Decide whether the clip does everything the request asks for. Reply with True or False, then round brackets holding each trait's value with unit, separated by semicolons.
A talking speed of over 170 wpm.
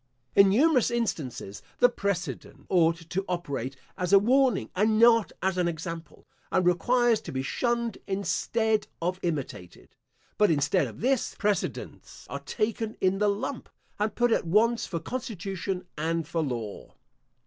False (150 wpm)